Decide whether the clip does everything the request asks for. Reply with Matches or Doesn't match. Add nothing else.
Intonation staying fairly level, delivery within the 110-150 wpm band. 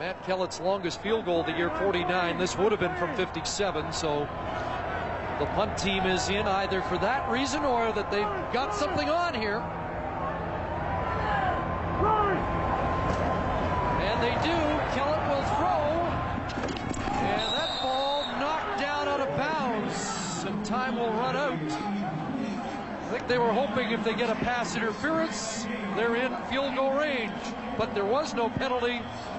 Doesn't match